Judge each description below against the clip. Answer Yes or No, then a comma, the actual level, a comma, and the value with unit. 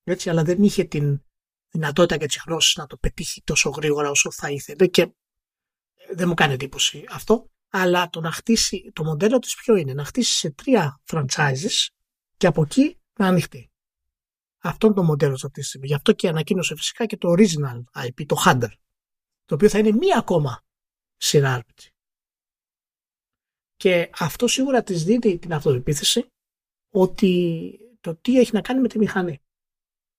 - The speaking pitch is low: No, medium, 175 Hz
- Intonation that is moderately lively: No, wide, 5.7 semitones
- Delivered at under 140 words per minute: No, average, 165 wpm